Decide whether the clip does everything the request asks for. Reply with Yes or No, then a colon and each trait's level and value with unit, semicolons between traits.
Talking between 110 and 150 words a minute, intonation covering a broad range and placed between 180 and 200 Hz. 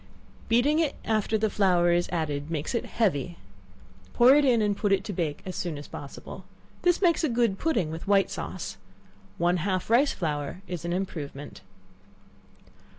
No: average, 170 wpm; wide, 5.8 semitones; high, 190 Hz